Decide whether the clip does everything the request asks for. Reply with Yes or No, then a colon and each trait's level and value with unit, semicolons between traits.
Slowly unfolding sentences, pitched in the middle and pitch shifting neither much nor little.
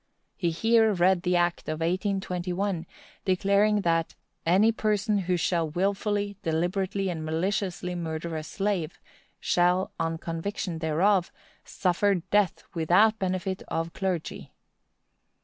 Yes: slow, 115 wpm; medium, 180 Hz; average, 3.0 semitones